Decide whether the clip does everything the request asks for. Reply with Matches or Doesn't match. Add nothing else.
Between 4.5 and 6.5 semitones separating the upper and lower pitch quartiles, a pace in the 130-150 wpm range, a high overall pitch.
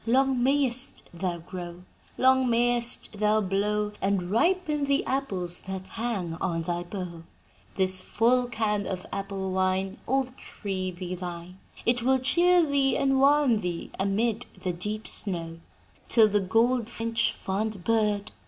Matches